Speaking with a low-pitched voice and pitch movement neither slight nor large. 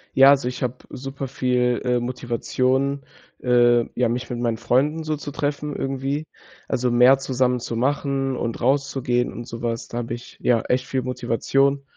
No: low, 125 Hz; narrow, 2.1 semitones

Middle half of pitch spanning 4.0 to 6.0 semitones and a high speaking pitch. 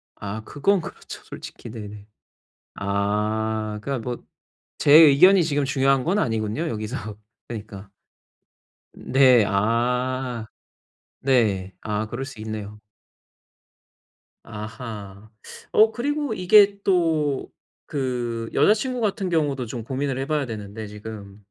No: average, 5.3 semitones; low, 120 Hz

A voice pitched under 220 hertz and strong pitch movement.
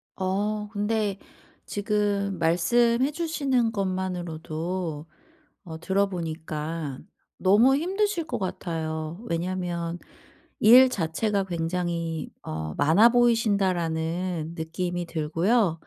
No: medium, 185 Hz; average, 4.5 semitones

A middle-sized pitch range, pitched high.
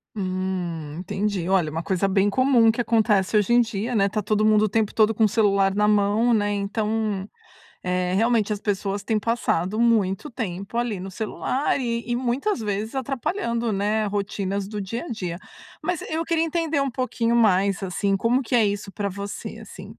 Yes: average, 3.0 semitones; high, 210 Hz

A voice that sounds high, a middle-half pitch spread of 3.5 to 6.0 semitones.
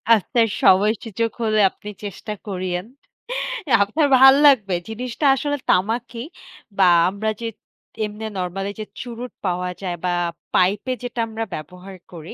Yes: high, 210 Hz; average, 3.8 semitones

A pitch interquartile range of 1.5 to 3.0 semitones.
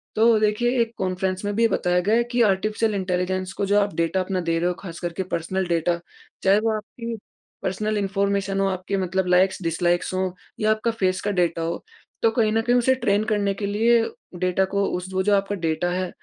Yes: average, 2.7 semitones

